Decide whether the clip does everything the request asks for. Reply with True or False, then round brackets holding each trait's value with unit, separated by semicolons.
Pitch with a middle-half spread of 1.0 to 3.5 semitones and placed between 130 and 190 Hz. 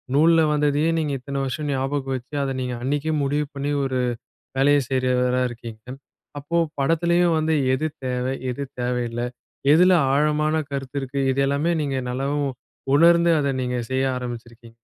True (2.9 semitones; 140 Hz)